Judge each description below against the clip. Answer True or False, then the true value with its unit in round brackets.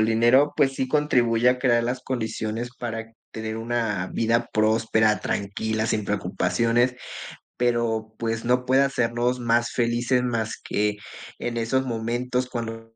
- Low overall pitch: True (115 Hz)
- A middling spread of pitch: False (1.8 semitones)